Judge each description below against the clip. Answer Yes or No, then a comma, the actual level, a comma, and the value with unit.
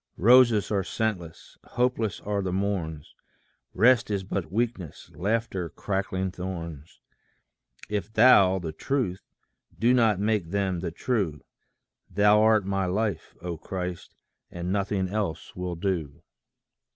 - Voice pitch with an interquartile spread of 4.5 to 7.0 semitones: No, average, 3.3 semitones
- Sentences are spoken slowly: Yes, slow, 125 wpm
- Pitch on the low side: Yes, very low, 95 Hz